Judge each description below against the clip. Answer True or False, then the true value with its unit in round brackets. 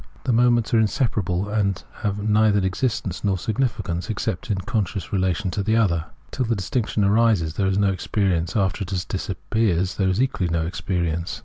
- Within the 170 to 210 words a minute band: True (180 wpm)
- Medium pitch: False (100 Hz)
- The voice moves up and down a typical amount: True (3.3 semitones)